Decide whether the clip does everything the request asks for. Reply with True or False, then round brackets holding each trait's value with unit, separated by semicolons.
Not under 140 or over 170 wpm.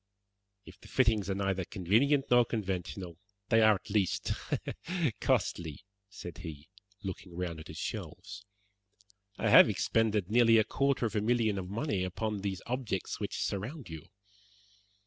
True (145 wpm)